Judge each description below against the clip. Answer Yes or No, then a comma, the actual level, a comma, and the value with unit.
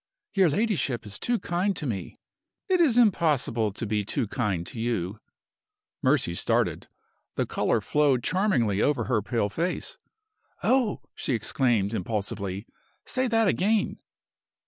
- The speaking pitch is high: No, low, 125 Hz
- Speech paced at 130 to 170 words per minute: Yes, slow, 135 wpm